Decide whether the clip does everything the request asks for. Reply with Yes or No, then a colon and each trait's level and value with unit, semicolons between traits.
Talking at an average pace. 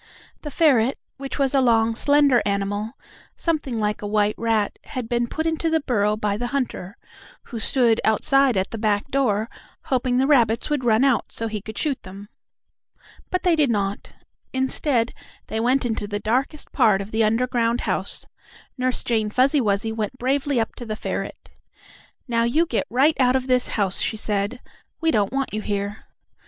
Yes: average, 180 wpm